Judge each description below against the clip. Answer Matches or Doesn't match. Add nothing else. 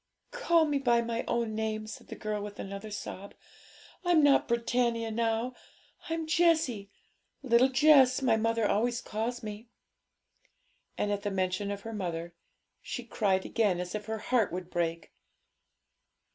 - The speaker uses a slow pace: Doesn't match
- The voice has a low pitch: Doesn't match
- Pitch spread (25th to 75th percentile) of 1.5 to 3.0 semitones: Doesn't match